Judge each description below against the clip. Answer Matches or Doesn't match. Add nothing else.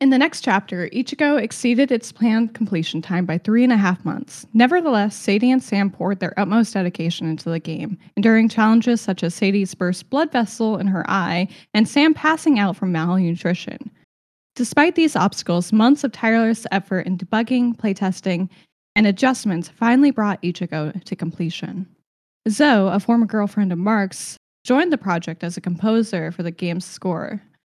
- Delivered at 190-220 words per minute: Doesn't match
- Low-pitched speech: Doesn't match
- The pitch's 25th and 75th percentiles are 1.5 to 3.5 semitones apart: Doesn't match